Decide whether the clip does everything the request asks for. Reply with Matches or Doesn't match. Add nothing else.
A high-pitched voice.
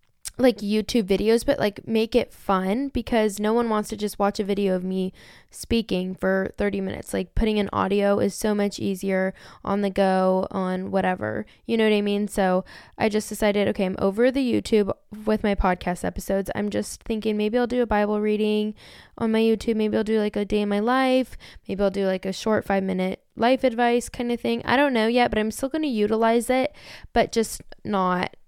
Matches